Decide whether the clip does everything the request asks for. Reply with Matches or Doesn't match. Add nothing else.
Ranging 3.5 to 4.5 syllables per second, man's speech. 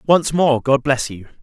Matches